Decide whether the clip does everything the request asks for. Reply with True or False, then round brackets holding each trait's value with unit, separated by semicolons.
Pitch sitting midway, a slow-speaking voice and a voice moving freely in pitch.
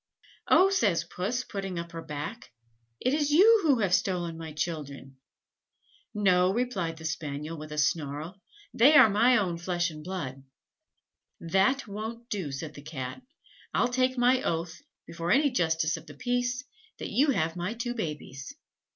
False (180 Hz; 160 wpm; 7.3 semitones)